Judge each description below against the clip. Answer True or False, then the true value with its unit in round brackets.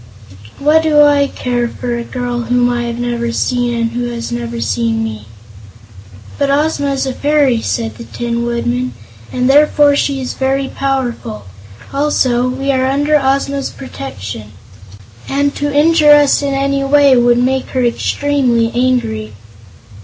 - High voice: True (255 Hz)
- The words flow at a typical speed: True (155 wpm)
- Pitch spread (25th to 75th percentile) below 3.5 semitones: True (3.0 semitones)